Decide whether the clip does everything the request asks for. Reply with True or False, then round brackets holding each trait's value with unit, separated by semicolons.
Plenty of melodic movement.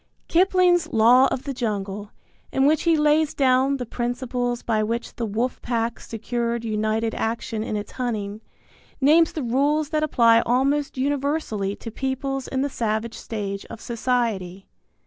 False (3.9 semitones)